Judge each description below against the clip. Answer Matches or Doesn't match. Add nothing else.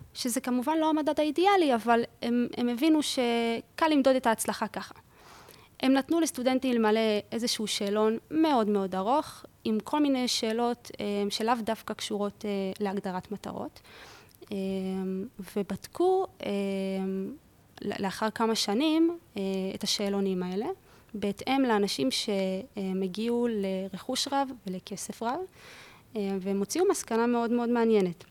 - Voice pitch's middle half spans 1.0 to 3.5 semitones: Doesn't match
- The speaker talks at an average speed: Doesn't match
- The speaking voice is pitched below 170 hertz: Doesn't match